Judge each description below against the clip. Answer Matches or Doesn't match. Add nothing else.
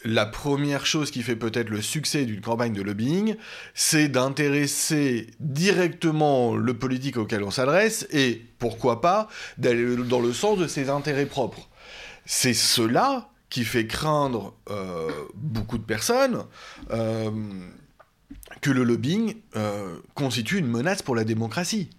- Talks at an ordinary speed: Doesn't match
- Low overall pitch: Matches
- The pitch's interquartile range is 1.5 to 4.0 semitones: Doesn't match